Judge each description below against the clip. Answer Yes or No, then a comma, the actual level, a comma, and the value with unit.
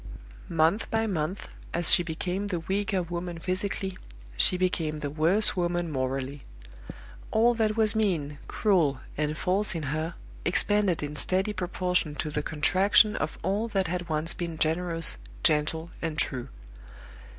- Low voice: No, medium, 175 Hz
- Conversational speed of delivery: Yes, average, 145 wpm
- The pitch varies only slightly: No, average, 3.8 semitones